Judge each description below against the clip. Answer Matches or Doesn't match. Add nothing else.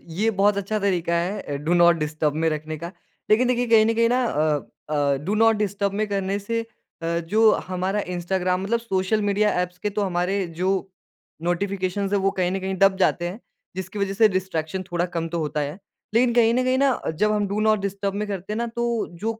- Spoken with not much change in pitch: Doesn't match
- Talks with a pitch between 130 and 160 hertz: Doesn't match